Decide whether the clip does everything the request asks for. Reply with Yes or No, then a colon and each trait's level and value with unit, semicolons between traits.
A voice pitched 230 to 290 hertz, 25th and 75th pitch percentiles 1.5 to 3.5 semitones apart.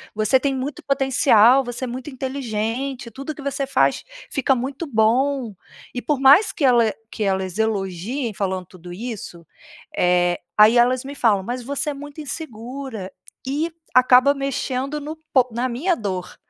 No: very high, 255 Hz; average, 4.2 semitones